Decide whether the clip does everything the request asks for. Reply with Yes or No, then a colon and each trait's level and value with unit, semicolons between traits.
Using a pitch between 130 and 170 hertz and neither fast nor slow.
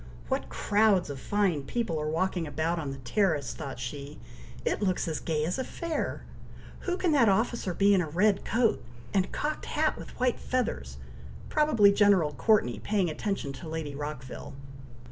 No: medium, 180 Hz; average, 170 wpm